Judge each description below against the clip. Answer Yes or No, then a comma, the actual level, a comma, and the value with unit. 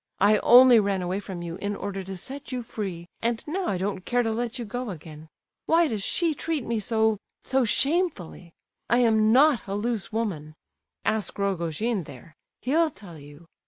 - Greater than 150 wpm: Yes, average, 175 wpm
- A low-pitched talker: No, high, 215 Hz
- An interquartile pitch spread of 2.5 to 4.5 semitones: No, average, 5.1 semitones